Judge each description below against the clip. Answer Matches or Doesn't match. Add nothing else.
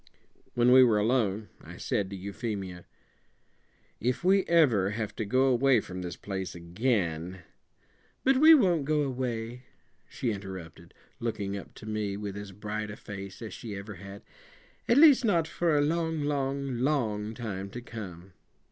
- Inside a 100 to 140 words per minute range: Doesn't match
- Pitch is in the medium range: Doesn't match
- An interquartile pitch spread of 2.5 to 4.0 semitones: Doesn't match